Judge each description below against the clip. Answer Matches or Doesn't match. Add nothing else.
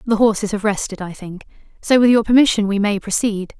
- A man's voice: Doesn't match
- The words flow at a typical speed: Doesn't match